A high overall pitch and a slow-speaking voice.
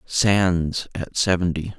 No: very low, 90 Hz; slow, 100 wpm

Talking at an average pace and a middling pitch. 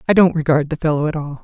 No: fast, 295 wpm; medium, 155 Hz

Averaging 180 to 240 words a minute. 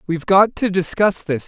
Yes: fast, 205 wpm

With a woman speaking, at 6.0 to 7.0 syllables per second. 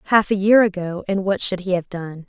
No: female; 5.5 syllables/s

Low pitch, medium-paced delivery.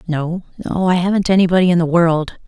No: medium, 175 Hz; average, 170 wpm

